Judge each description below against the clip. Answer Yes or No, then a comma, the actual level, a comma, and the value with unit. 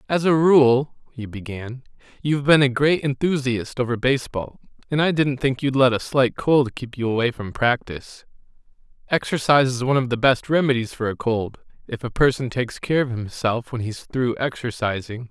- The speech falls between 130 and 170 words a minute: No, average, 185 wpm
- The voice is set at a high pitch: No, low, 125 Hz